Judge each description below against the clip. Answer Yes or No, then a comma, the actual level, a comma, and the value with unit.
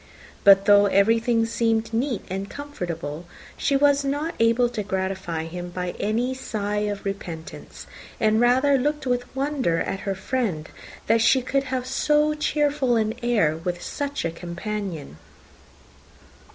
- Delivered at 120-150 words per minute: Yes, average, 140 wpm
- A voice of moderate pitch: No, high, 225 Hz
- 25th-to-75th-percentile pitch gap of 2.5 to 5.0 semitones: No, wide, 5.6 semitones